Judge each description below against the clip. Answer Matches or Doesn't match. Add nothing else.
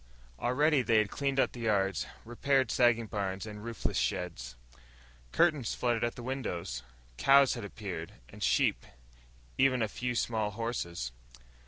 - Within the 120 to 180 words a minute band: Matches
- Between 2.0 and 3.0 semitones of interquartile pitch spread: Doesn't match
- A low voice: Matches